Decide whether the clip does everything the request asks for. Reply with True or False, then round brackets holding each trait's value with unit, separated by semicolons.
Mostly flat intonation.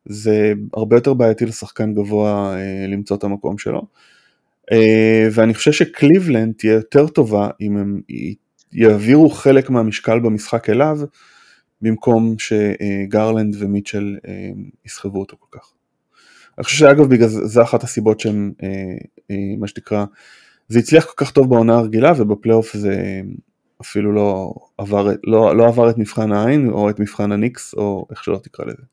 True (2.3 semitones)